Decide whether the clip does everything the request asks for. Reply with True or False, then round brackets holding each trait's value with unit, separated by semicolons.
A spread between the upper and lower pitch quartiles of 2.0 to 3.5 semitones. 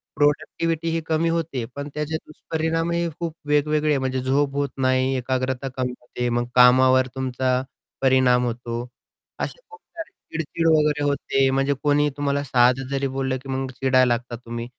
True (2.9 semitones)